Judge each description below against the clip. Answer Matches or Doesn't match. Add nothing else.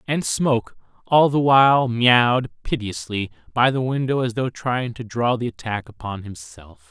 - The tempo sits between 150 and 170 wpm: Matches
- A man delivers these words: Matches